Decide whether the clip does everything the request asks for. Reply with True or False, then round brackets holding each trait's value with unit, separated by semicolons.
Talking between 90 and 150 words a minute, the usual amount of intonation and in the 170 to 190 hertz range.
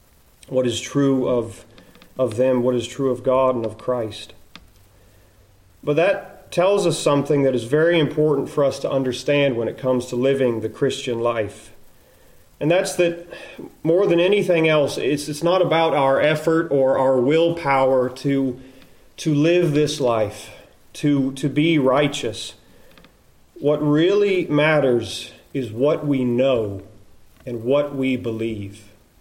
False (145 wpm; 4.0 semitones; 135 Hz)